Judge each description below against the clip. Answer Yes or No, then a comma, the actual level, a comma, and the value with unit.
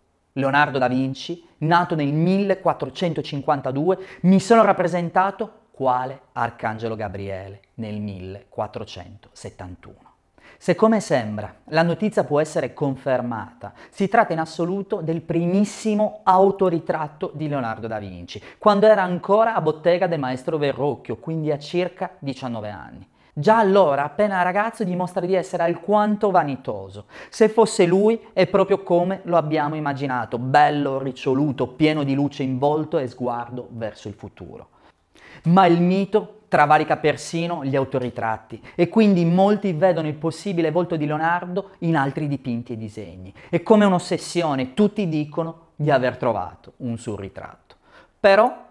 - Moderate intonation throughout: No, wide, 6.7 semitones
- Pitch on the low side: No, medium, 155 Hz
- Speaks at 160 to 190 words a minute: No, average, 135 wpm